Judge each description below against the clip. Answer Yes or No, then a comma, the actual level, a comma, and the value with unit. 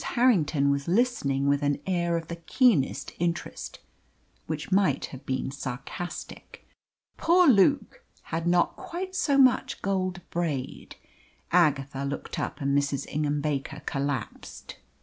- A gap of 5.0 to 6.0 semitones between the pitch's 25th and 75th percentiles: Yes, wide, 5.4 semitones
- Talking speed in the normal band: No, slow, 130 wpm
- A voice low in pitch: No, medium, 160 Hz